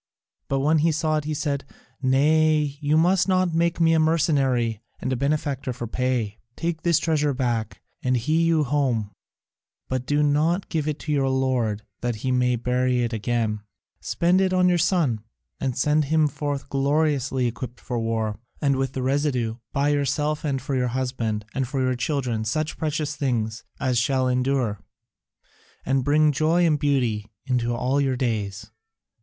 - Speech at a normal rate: Yes, average, 170 wpm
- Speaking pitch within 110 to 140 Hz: Yes, low, 135 Hz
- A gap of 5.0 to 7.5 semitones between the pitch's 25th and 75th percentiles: No, average, 3.8 semitones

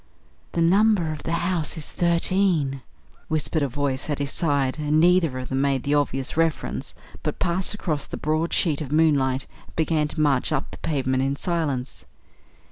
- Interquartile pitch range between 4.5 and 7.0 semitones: No, average, 3.3 semitones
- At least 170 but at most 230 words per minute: Yes, average, 180 wpm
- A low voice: No, medium, 150 Hz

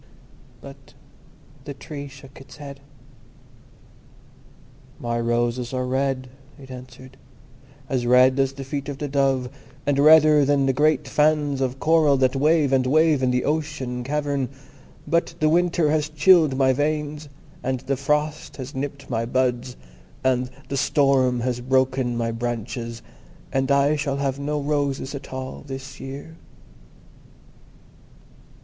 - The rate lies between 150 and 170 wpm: No, average, 140 wpm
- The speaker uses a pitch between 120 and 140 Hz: Yes, low, 135 Hz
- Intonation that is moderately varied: No, narrow, 2.3 semitones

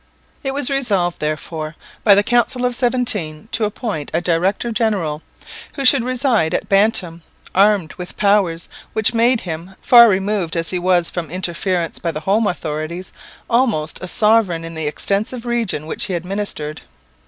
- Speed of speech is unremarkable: Yes, average, 160 wpm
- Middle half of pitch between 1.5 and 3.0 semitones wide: No, wide, 5.5 semitones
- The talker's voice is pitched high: Yes, high, 195 Hz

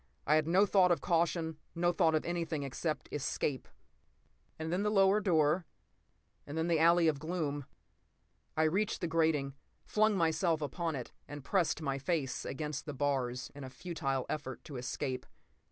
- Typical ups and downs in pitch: Yes, average, 3.3 semitones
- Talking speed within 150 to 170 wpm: Yes, average, 165 wpm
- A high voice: No, medium, 160 Hz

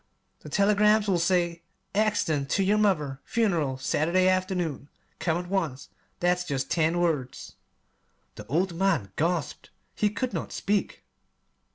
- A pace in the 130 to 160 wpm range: Yes, slow, 135 wpm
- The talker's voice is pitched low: No, medium, 175 Hz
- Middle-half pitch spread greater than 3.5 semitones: Yes, average, 3.9 semitones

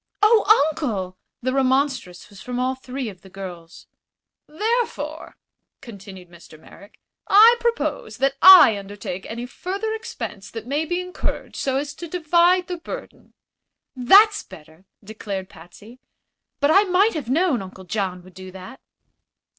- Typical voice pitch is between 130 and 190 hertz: No, very high, 255 Hz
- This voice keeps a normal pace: Yes, average, 145 wpm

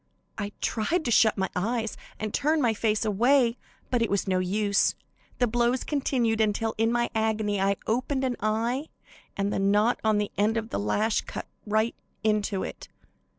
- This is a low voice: No, high, 220 Hz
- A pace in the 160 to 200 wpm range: Yes, average, 180 wpm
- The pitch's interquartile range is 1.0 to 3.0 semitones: Yes, narrow, 2.5 semitones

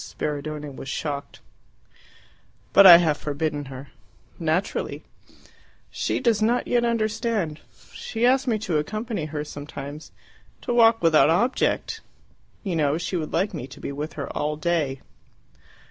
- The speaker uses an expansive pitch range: Yes, wide, 6.7 semitones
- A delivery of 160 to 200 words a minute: No, average, 140 wpm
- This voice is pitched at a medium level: Yes, medium, 160 Hz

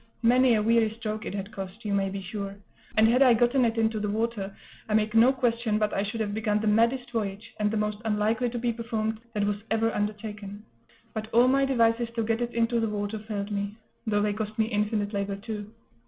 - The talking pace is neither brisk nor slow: No, fast, 230 wpm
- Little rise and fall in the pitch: Yes, narrow, 1.8 semitones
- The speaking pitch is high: Yes, high, 220 Hz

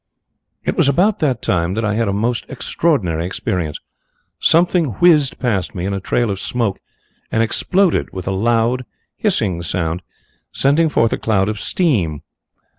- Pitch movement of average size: No, wide, 6.8 semitones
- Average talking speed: Yes, average, 160 wpm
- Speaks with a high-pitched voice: No, low, 115 Hz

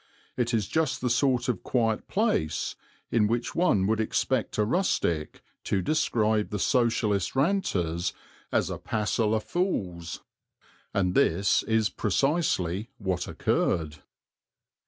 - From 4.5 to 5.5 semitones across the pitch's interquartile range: Yes, average, 5.0 semitones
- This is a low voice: Yes, low, 110 Hz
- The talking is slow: Yes, slow, 125 wpm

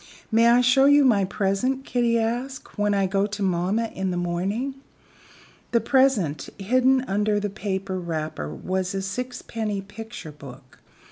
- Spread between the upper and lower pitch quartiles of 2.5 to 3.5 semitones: No, average, 4.2 semitones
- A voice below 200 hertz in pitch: No, high, 205 Hz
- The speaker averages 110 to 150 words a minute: Yes, average, 145 wpm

